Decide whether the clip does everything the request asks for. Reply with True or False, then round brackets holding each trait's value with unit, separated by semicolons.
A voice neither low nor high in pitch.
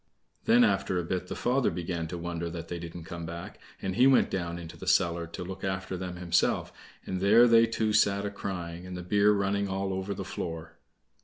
False (90 Hz)